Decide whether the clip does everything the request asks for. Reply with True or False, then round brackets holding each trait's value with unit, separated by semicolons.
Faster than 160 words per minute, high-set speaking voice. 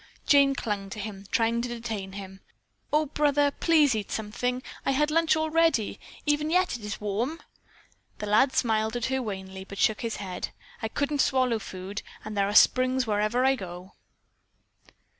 True (175 wpm; 230 Hz)